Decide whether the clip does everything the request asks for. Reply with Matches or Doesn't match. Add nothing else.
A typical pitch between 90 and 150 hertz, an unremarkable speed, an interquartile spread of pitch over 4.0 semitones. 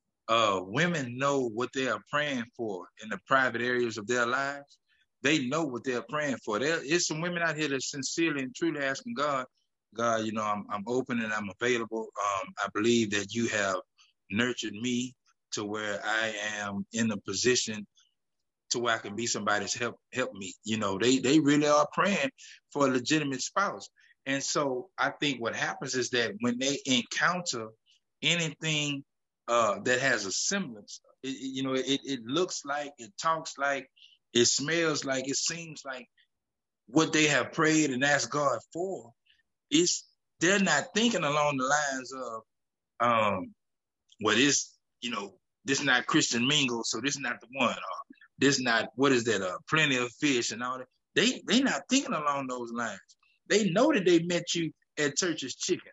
Matches